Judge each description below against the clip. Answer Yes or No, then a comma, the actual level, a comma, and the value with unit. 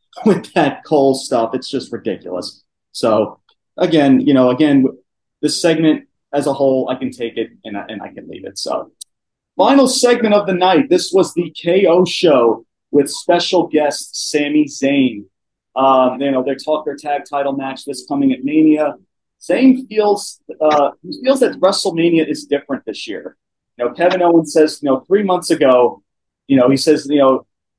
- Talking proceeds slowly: No, average, 180 wpm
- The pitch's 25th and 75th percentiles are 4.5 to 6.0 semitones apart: Yes, average, 5.1 semitones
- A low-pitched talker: No, medium, 150 Hz